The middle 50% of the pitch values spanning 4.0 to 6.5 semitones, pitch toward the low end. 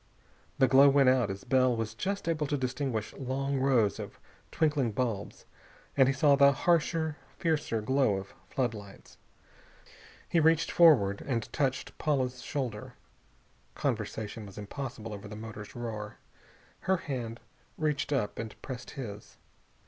Yes: average, 4.4 semitones; low, 130 Hz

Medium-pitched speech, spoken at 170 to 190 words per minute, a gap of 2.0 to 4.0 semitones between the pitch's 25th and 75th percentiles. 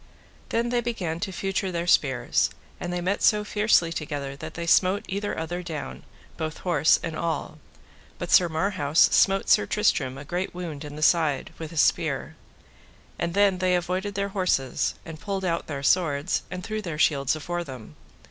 Yes: medium, 175 Hz; average, 180 wpm; average, 3.7 semitones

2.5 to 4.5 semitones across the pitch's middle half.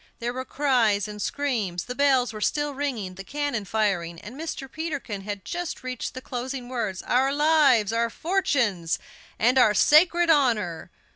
No: wide, 5.6 semitones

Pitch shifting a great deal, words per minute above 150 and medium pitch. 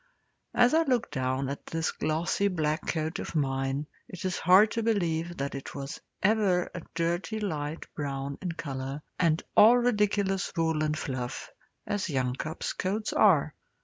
Yes: wide, 5.8 semitones; average, 160 wpm; medium, 165 Hz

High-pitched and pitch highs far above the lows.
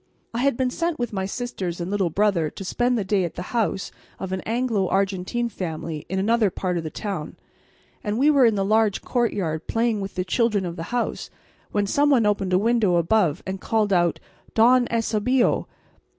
No: high, 205 Hz; average, 4.2 semitones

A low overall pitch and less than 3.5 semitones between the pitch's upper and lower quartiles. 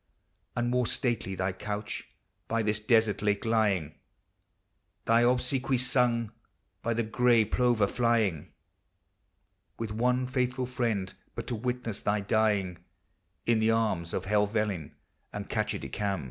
Yes: low, 110 Hz; average, 2.9 semitones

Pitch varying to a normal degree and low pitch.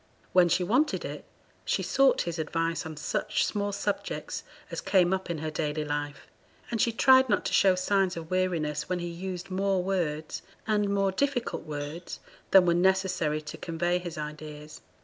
No: average, 3.8 semitones; medium, 180 Hz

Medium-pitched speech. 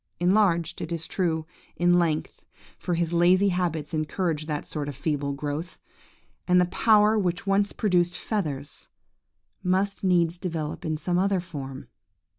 Yes: medium, 175 Hz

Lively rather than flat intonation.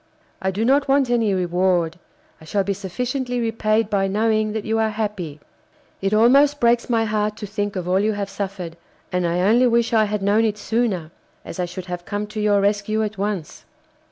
No: average, 2.8 semitones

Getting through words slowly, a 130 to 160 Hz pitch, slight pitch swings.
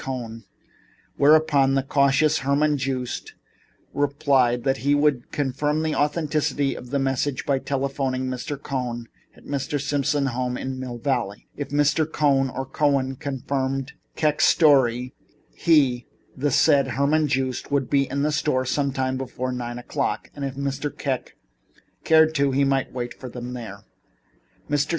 No: average, 155 wpm; low, 135 Hz; narrow, 2.0 semitones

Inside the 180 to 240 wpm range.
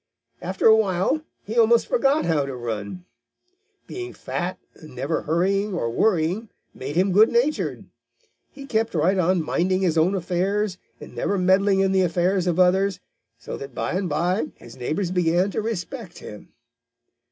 No: average, 165 wpm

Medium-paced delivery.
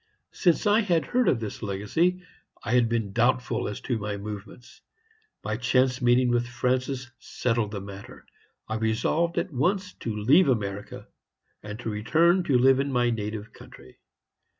Yes: average, 160 wpm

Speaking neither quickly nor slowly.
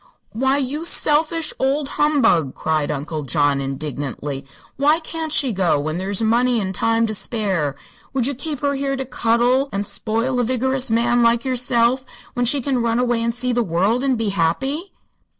Yes: average, 180 wpm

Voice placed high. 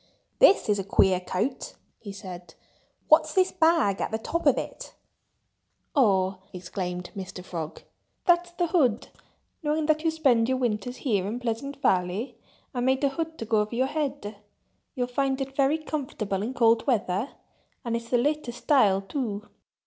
Yes: high, 245 Hz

